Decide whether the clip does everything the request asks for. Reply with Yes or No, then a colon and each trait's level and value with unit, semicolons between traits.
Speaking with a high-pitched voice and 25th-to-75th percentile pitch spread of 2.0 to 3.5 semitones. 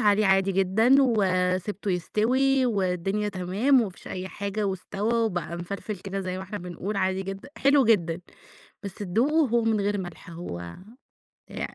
Yes: high, 195 Hz; average, 3.2 semitones